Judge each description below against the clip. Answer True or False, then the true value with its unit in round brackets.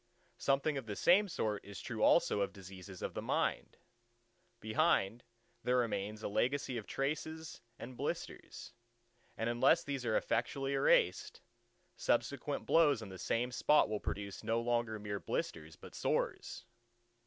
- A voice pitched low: True (120 Hz)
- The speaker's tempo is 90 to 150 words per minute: True (145 wpm)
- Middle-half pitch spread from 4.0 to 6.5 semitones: True (5.2 semitones)